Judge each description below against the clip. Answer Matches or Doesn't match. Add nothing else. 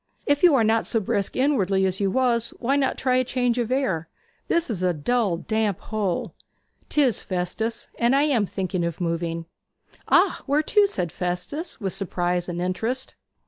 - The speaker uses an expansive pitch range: Matches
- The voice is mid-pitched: Doesn't match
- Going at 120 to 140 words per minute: Doesn't match